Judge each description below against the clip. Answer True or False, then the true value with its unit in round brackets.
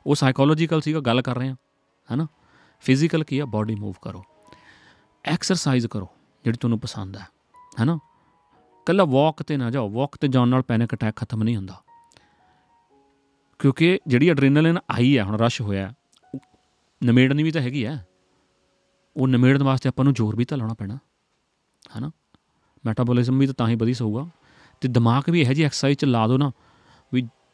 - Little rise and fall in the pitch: False (3.8 semitones)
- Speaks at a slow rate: False (165 wpm)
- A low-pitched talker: True (130 Hz)